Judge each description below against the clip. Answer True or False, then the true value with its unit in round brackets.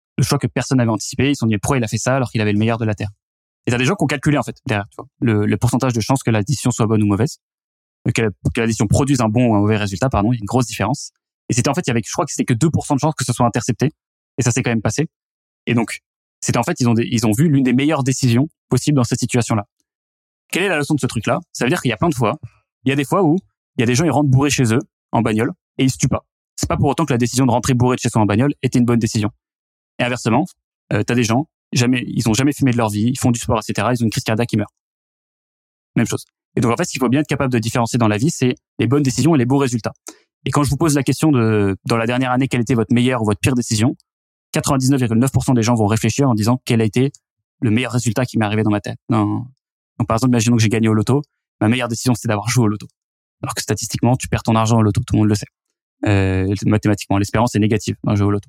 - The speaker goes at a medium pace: False (300 wpm)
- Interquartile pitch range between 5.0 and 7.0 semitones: False (3.3 semitones)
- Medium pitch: False (120 Hz)